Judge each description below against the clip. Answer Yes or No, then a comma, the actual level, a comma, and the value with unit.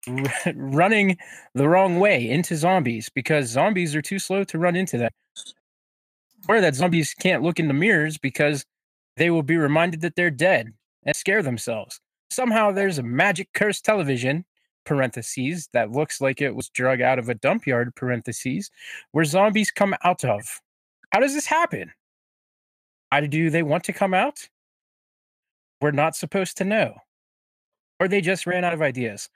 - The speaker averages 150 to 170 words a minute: Yes, average, 165 wpm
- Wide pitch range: Yes, wide, 5.8 semitones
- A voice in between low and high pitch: Yes, medium, 165 Hz